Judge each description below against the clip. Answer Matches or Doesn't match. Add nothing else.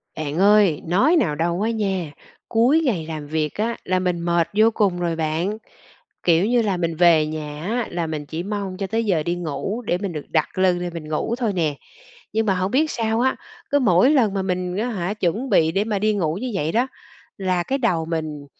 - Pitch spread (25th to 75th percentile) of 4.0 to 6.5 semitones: Matches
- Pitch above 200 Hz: Doesn't match